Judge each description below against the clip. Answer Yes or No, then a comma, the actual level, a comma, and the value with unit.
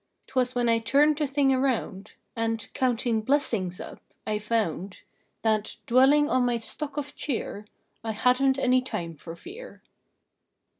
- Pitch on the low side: No, high, 245 Hz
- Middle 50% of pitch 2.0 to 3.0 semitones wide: No, average, 3.9 semitones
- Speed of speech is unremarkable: Yes, average, 150 wpm